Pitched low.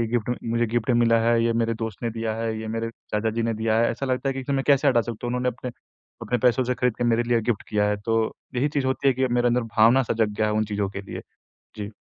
Yes: low, 115 Hz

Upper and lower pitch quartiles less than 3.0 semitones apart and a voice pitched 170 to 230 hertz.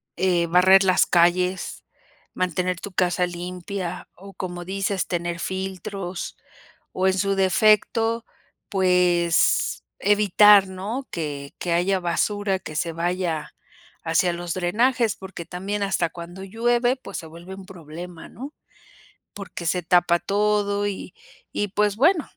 Yes: narrow, 2.5 semitones; medium, 185 Hz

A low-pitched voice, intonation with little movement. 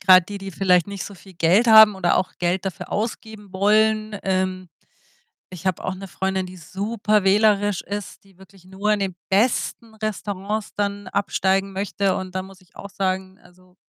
No: high, 195 Hz; narrow, 1.8 semitones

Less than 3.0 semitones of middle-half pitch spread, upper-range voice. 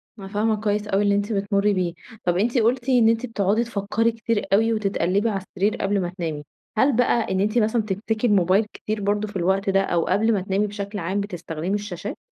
Yes: narrow, 2.4 semitones; high, 205 Hz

